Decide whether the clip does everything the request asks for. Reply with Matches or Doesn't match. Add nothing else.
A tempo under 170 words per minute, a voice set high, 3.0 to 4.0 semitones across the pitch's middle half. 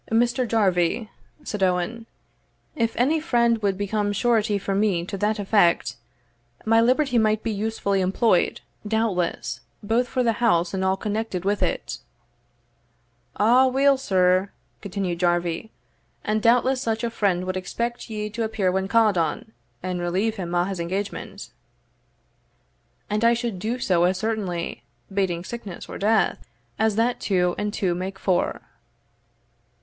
Matches